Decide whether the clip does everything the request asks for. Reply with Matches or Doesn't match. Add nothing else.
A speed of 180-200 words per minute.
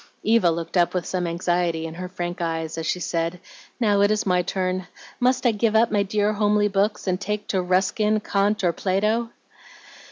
Matches